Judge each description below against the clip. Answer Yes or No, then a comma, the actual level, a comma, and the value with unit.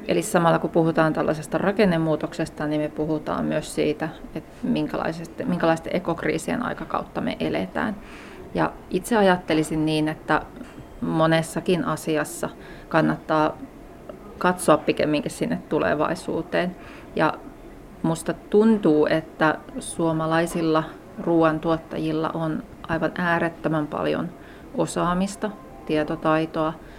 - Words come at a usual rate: No, slow, 90 wpm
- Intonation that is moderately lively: No, narrow, 1.5 semitones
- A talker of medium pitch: Yes, medium, 160 Hz